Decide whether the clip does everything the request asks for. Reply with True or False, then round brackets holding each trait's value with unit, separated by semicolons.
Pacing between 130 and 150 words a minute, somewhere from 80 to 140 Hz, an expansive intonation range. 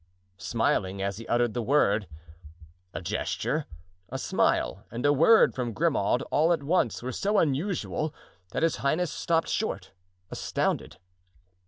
True (140 wpm; 135 Hz; 6.6 semitones)